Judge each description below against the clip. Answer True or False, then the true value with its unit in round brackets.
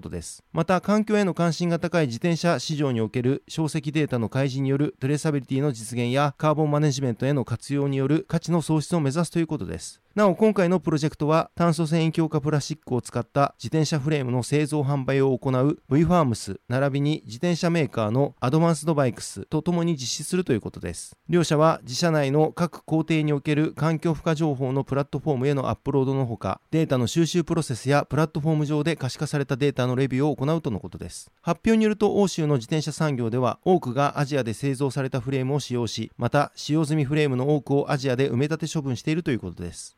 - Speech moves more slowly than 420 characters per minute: False (480 characters per minute)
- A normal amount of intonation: True (3.5 semitones)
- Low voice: False (145 Hz)